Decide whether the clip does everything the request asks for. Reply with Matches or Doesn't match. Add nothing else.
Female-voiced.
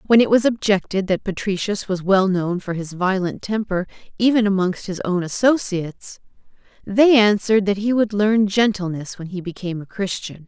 Matches